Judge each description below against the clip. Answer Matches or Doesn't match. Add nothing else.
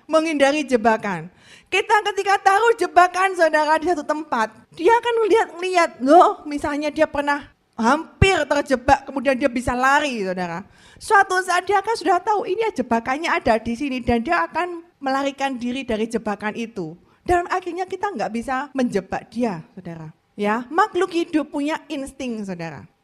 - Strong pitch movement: Matches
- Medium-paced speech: Doesn't match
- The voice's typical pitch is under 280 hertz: Doesn't match